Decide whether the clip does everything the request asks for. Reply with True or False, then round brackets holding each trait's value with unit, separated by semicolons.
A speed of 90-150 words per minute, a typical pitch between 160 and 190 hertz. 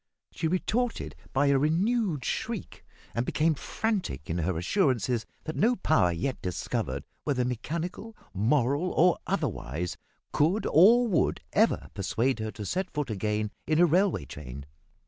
False (145 wpm; 140 Hz)